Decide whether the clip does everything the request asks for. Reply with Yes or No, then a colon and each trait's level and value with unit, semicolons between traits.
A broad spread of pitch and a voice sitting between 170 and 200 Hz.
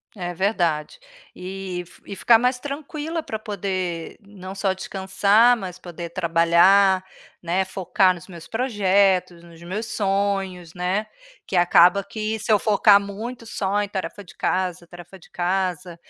No: narrow, 2.6 semitones; high, 190 Hz